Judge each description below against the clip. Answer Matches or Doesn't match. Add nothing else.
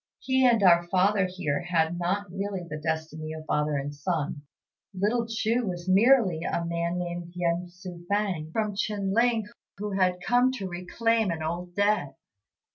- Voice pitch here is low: Doesn't match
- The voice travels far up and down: Doesn't match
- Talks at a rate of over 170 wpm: Doesn't match